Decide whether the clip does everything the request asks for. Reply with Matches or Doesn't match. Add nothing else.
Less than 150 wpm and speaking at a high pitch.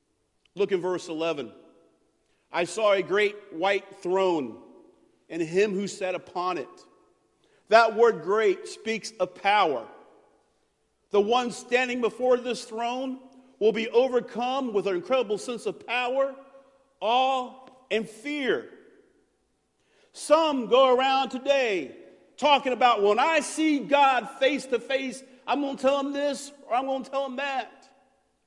Matches